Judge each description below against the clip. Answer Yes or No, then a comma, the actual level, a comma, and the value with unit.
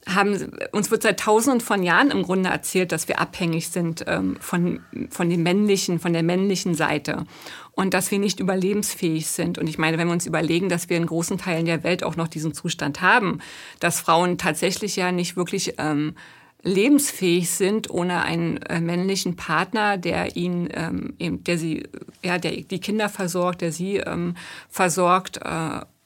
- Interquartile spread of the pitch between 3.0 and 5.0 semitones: No, narrow, 2.5 semitones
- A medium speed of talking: Yes, average, 180 wpm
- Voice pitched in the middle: Yes, medium, 175 Hz